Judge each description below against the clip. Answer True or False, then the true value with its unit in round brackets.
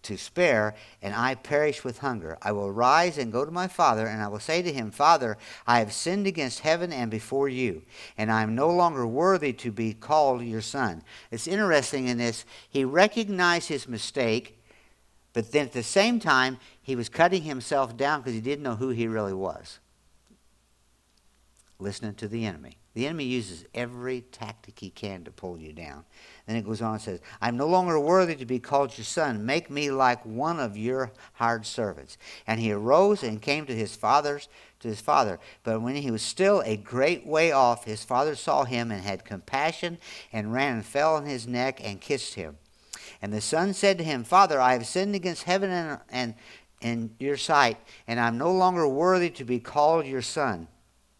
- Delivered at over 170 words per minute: True (200 wpm)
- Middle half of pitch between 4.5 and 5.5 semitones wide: True (5.1 semitones)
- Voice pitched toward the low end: True (125 Hz)